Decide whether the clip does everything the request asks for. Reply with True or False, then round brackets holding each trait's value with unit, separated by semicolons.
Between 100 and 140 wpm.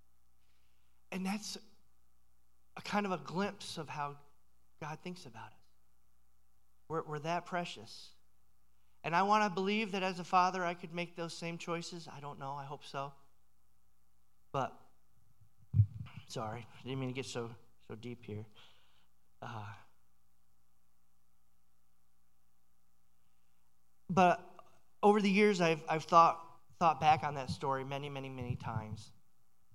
True (135 wpm)